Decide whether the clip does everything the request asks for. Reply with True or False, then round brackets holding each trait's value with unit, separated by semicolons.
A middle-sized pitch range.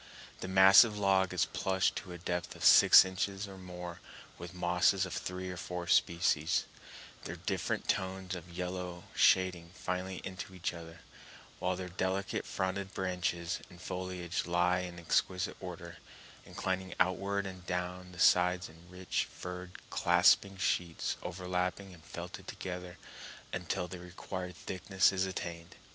False (1.1 semitones)